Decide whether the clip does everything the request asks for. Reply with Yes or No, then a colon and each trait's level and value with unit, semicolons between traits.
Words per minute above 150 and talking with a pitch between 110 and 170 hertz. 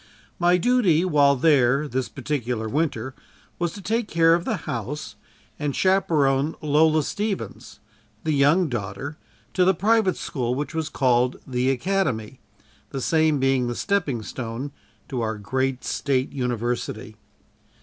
No: average, 140 wpm; medium, 140 Hz